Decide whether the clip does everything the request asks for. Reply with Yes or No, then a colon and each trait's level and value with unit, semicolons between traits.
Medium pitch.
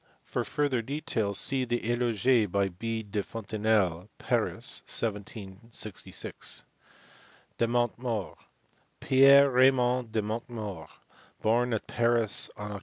No: low, 115 Hz